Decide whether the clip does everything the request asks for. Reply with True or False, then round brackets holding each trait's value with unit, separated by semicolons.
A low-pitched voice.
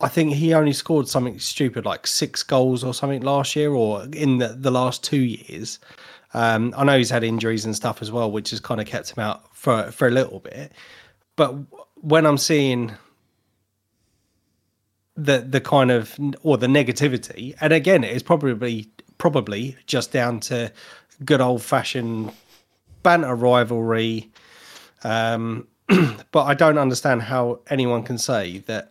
True (125 Hz)